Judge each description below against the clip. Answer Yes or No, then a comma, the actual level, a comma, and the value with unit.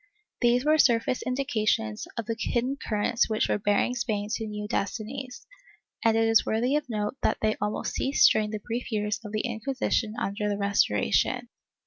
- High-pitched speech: Yes, high, 220 Hz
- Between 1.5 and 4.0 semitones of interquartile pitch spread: Yes, average, 3.0 semitones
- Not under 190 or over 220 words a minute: No, average, 180 wpm